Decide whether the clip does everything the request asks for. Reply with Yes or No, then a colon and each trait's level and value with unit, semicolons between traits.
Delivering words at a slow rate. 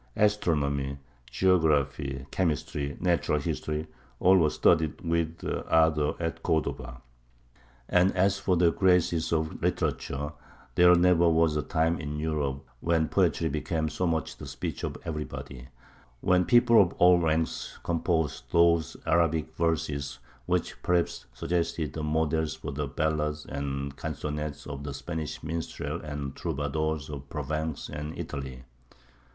Yes: slow, 130 wpm